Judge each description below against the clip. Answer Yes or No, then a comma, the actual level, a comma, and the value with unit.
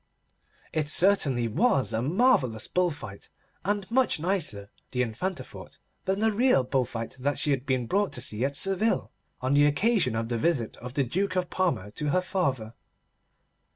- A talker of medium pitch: Yes, medium, 145 Hz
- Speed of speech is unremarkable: Yes, average, 180 wpm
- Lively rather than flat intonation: Yes, wide, 7.6 semitones